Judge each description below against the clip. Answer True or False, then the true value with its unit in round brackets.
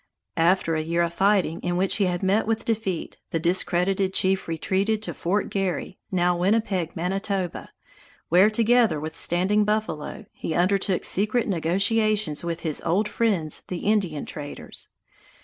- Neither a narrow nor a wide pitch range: True (3.5 semitones)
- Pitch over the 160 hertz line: True (190 Hz)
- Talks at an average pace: True (150 wpm)